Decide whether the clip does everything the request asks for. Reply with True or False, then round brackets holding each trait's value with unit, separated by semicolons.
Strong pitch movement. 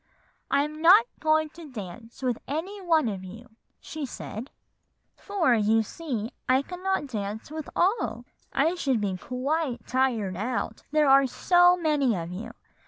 True (6.0 semitones)